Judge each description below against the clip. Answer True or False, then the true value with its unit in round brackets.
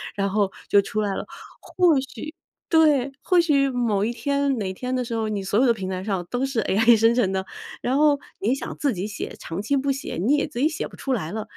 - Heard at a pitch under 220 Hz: False (235 Hz)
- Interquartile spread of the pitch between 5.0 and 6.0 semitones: True (5.3 semitones)